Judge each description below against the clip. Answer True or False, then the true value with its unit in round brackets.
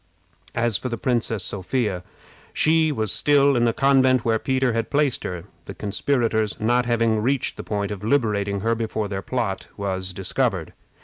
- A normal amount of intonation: True (4.0 semitones)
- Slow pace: False (170 wpm)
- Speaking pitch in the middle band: False (115 Hz)